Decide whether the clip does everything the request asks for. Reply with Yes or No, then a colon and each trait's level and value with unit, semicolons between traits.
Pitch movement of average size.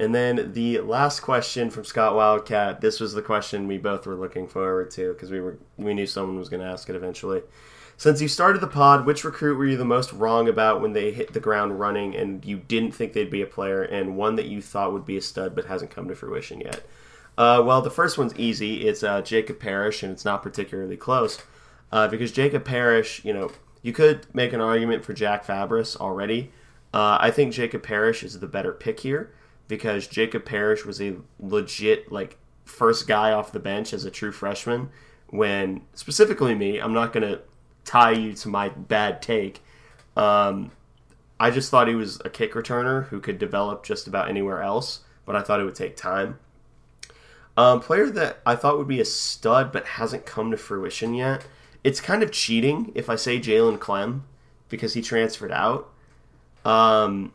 Yes: average, 4.4 semitones